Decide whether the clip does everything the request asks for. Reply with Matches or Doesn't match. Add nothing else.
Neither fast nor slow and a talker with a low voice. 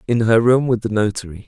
Doesn't match